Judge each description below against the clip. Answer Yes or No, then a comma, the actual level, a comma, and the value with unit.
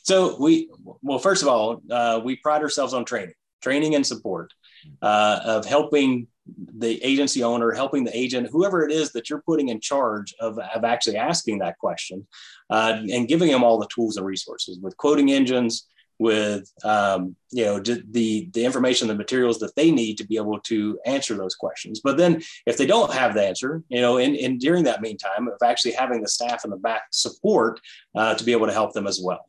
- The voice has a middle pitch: No, low, 120 Hz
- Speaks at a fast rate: Yes, fast, 210 wpm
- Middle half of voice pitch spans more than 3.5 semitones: Yes, average, 4.1 semitones